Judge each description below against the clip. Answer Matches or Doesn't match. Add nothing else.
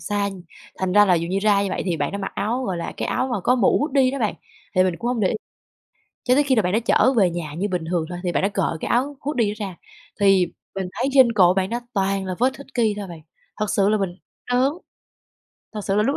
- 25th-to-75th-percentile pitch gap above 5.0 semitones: Doesn't match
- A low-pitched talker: Doesn't match